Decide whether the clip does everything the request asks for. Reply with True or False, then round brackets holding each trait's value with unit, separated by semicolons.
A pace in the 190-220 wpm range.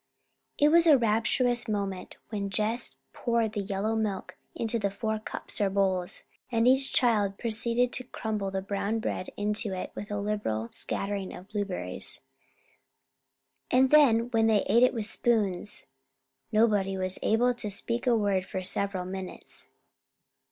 False (150 wpm)